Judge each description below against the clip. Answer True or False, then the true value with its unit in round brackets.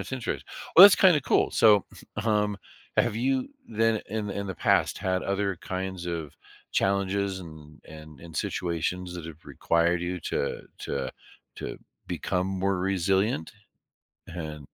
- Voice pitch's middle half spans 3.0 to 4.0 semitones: True (3.4 semitones)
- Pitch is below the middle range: True (95 Hz)